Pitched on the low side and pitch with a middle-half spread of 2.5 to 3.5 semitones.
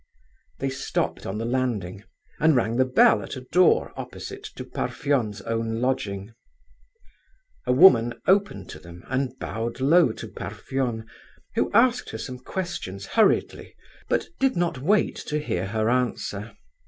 No: low, 125 Hz; average, 5.3 semitones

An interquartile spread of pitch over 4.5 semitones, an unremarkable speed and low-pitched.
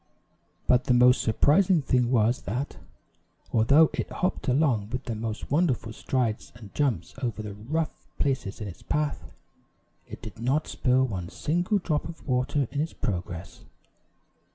Yes: average, 5.0 semitones; average, 155 wpm; low, 125 Hz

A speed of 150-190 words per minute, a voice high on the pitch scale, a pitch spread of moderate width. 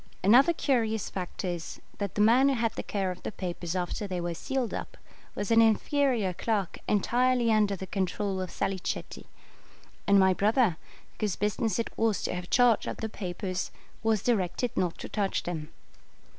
Yes: average, 175 wpm; high, 205 Hz; average, 3.7 semitones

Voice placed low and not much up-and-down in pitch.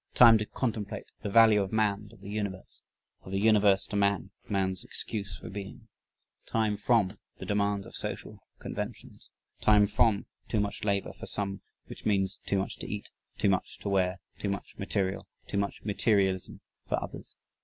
Yes: low, 100 Hz; narrow, 1.4 semitones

